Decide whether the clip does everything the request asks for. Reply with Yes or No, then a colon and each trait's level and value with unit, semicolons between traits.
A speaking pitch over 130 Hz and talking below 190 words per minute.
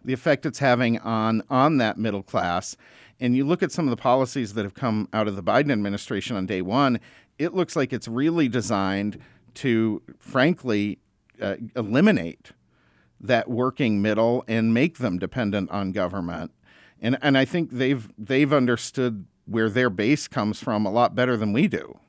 No: low, 115 Hz; average, 175 wpm